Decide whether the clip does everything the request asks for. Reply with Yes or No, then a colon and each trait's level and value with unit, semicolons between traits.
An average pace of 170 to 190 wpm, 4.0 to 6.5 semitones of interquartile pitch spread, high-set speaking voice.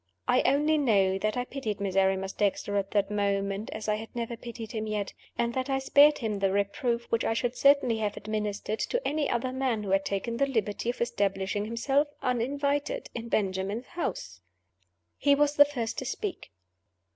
Yes: average, 185 wpm; average, 4.8 semitones; high, 225 Hz